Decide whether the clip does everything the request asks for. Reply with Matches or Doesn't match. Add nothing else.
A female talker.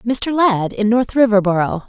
Matches